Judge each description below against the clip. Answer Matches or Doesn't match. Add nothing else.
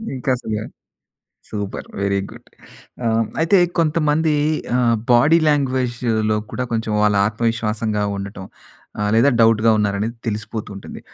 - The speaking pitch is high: Doesn't match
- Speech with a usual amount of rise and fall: Matches